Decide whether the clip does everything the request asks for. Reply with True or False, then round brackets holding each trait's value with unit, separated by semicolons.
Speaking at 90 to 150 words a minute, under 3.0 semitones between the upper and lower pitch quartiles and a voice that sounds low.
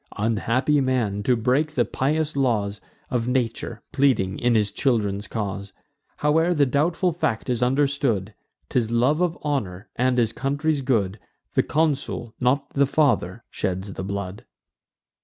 False (140 wpm; 5.1 semitones; 125 Hz)